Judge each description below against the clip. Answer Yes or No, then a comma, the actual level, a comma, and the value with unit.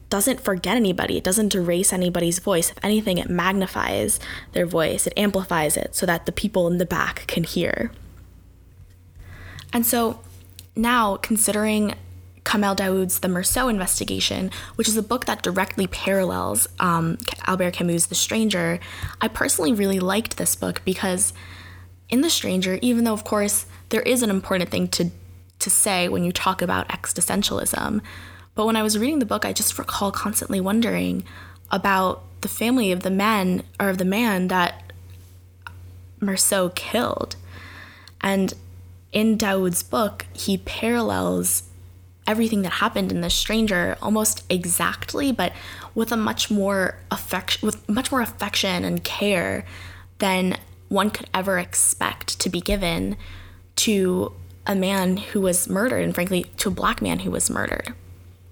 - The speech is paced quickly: No, average, 150 wpm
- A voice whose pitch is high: No, medium, 180 Hz